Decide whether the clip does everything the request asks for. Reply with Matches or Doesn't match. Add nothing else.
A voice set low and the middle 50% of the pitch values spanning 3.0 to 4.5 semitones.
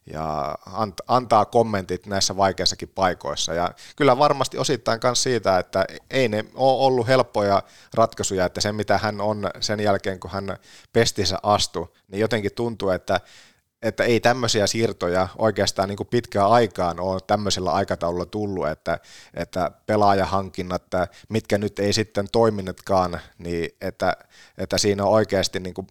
Doesn't match